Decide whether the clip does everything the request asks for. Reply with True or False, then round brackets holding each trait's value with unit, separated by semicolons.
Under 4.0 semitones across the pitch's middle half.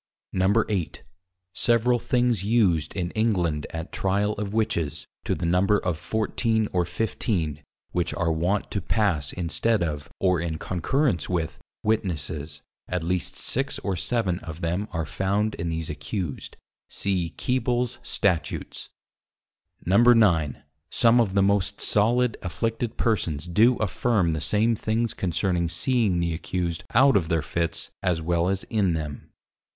False (4.8 semitones)